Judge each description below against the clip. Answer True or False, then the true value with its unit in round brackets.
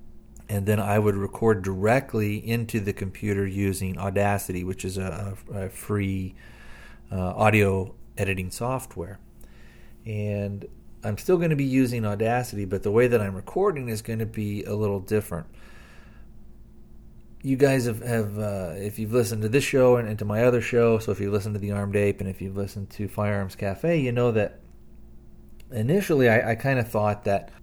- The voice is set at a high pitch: False (105 Hz)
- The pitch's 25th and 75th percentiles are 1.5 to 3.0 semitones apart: True (2.5 semitones)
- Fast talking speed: False (180 wpm)